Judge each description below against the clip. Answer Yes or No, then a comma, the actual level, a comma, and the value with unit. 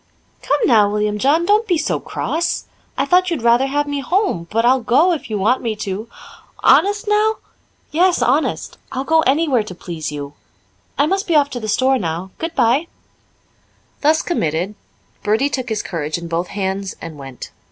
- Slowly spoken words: No, average, 180 wpm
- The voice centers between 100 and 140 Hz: No, very high, 250 Hz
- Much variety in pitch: Yes, wide, 8.3 semitones